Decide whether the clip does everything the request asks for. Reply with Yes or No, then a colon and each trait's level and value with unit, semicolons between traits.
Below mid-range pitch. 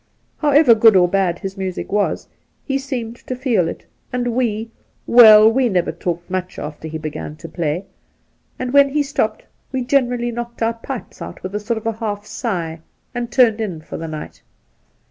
No: high, 220 Hz